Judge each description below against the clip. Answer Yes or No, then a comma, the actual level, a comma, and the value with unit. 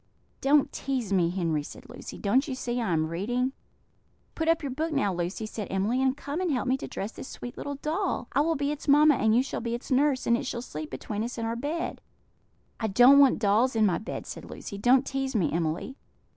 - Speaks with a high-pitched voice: Yes, high, 245 Hz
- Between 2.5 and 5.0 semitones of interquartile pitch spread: No, wide, 5.4 semitones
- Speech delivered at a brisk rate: Yes, fast, 235 wpm